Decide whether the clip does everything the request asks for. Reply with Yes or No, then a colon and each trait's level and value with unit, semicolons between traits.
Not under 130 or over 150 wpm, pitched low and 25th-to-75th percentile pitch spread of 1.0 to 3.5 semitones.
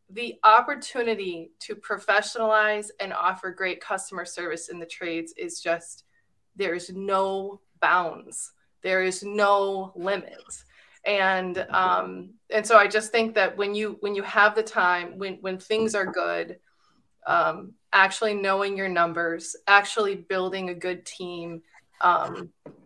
No: average, 140 wpm; high, 195 Hz; narrow, 2.4 semitones